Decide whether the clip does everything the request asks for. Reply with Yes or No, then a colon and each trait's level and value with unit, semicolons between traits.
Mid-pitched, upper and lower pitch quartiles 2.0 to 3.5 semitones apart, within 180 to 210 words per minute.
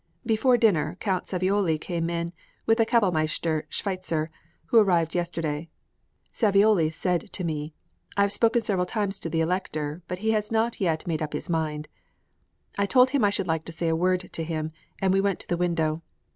No: medium, 180 Hz; average, 3.9 semitones; average, 190 wpm